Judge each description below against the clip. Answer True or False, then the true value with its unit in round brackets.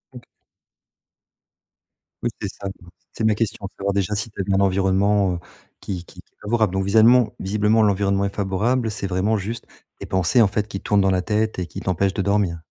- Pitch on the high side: False (100 Hz)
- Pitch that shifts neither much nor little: False (2.0 semitones)